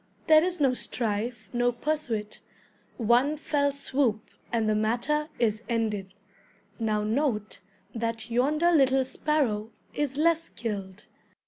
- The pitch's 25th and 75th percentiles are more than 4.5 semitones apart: Yes, average, 5.1 semitones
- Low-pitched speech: No, high, 240 Hz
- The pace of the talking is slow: Yes, slow, 120 wpm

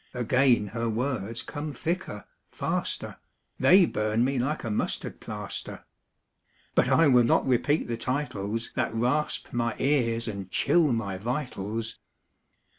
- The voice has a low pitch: Yes, low, 120 Hz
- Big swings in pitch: No, average, 3.8 semitones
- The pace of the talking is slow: Yes, slow, 130 wpm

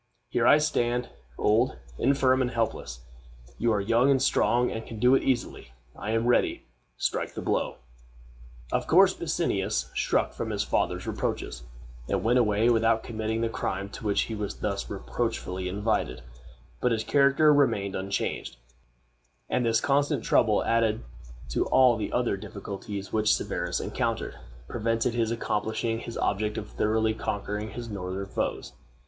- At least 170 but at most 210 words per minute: No, average, 155 wpm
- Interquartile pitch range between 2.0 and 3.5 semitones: Yes, average, 2.8 semitones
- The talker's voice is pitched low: Yes, low, 115 Hz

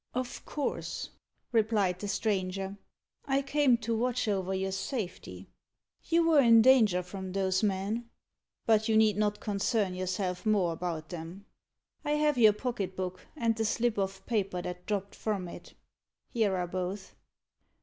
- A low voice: No, high, 205 Hz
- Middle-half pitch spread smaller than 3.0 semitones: No, average, 3.6 semitones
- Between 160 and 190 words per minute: No, average, 150 wpm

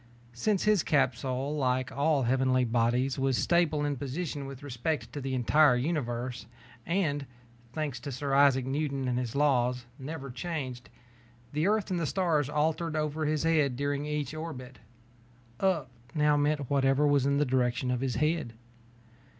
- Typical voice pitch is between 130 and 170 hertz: Yes, medium, 140 Hz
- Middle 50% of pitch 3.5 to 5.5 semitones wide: No, average, 3.0 semitones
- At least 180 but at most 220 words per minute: No, average, 160 wpm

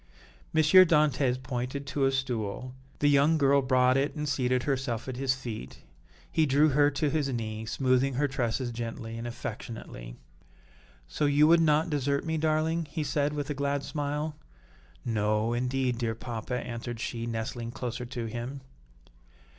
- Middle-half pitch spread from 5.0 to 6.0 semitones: No, average, 3.4 semitones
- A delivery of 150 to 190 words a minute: Yes, average, 160 wpm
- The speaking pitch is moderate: No, low, 130 Hz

